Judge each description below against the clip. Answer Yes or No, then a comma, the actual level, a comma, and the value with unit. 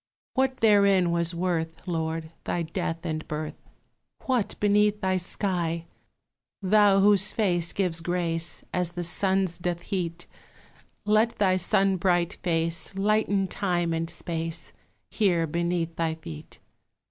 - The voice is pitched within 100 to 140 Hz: No, medium, 175 Hz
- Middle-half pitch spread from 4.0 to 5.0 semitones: No, average, 2.9 semitones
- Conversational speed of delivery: No, slow, 125 wpm